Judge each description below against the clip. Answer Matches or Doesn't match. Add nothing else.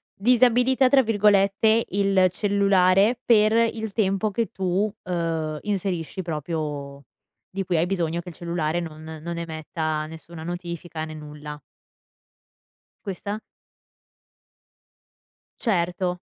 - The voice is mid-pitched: Matches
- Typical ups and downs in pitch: Matches